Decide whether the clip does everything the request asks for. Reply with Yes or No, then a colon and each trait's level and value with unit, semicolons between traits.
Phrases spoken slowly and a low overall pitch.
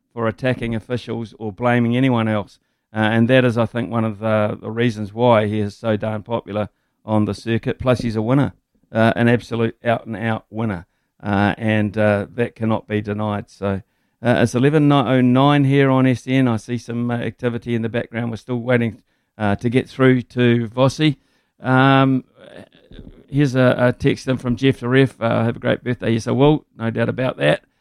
No: average, 200 wpm; low, 115 Hz